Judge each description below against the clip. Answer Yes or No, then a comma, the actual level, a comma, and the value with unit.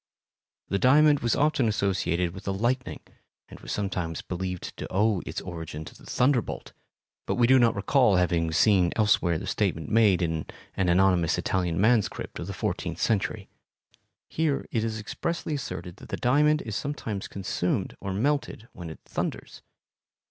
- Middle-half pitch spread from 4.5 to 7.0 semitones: Yes, average, 5.1 semitones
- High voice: No, low, 100 Hz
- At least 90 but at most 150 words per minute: No, average, 165 wpm